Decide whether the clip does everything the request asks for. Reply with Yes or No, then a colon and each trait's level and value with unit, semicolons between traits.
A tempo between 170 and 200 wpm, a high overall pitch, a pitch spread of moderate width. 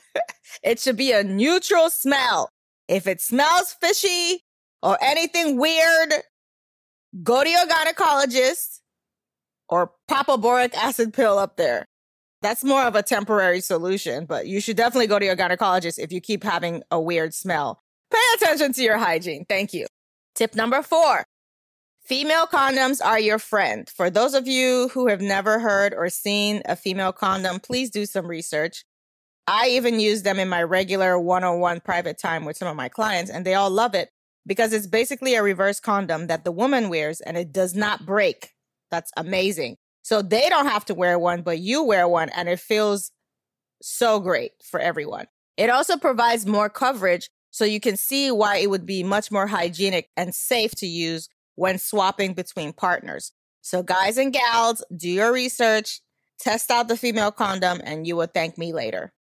No: average, 180 wpm; high, 210 Hz; wide, 5.7 semitones